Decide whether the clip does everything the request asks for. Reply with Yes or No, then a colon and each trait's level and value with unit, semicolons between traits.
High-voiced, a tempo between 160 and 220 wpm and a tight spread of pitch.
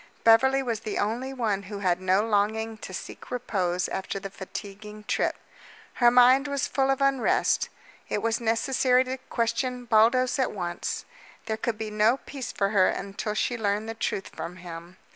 No: high, 220 Hz; average, 175 wpm; average, 3.8 semitones